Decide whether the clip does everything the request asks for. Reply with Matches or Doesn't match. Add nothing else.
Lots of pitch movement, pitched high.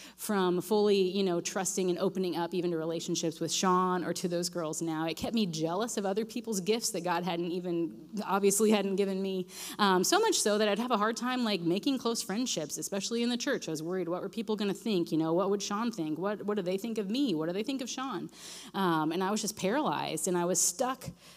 Doesn't match